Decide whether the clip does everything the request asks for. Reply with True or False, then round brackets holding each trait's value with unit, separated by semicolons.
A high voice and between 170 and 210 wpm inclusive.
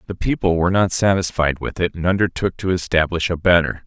False (90 Hz; 200 wpm)